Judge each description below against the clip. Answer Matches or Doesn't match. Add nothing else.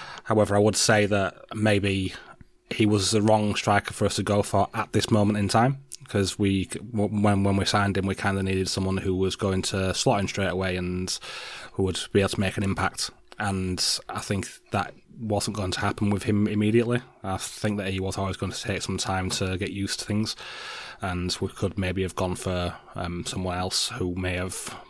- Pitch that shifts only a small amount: Matches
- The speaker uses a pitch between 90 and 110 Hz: Matches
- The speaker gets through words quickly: Matches